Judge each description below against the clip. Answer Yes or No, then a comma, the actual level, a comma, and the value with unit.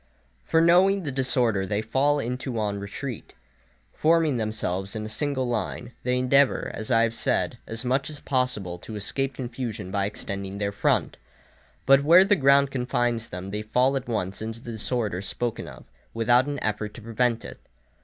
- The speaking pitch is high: No, low, 120 Hz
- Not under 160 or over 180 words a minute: Yes, average, 175 wpm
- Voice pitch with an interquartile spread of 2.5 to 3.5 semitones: No, average, 4.1 semitones